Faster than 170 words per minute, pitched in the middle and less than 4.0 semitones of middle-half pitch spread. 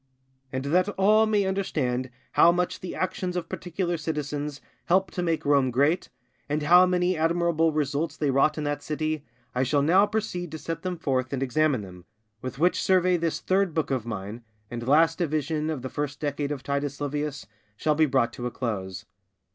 No: average, 190 wpm; medium, 150 Hz; average, 4.3 semitones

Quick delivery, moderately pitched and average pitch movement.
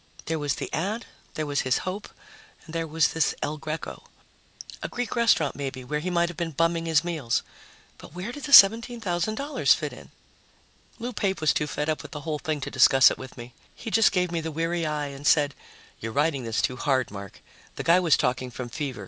Yes: fast, 215 wpm; medium, 160 Hz; average, 4.0 semitones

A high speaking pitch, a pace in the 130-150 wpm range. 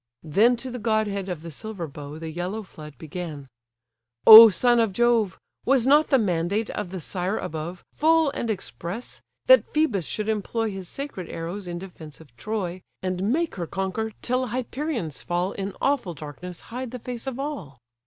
No: high, 200 Hz; average, 175 wpm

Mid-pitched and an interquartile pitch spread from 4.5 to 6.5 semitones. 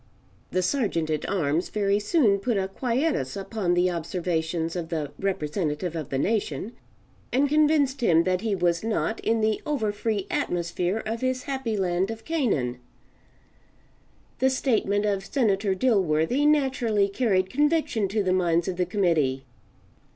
No: high, 200 Hz; average, 5.0 semitones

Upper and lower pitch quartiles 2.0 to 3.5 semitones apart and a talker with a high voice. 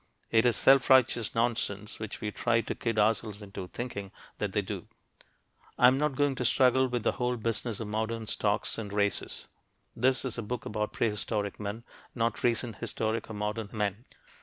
No: narrow, 2.6 semitones; low, 115 Hz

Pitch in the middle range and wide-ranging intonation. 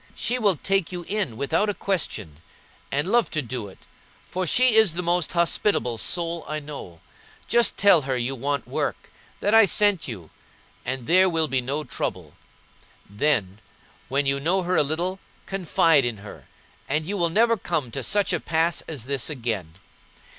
Yes: medium, 155 Hz; wide, 6.2 semitones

